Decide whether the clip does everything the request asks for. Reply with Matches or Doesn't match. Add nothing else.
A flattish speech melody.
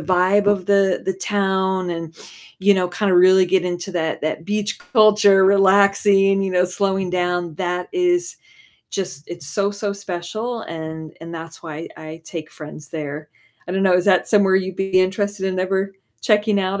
Matches